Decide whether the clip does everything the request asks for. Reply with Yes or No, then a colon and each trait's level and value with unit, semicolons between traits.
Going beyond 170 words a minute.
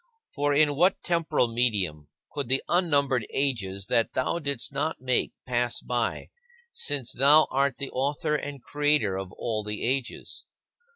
No: average, 150 wpm